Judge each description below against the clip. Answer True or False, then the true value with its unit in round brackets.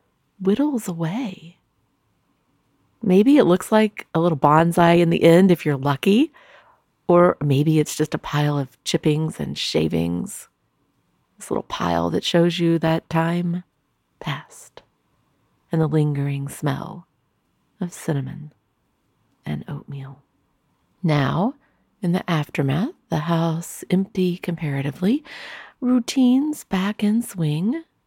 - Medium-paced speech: False (115 wpm)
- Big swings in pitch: False (4.6 semitones)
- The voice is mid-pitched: True (165 Hz)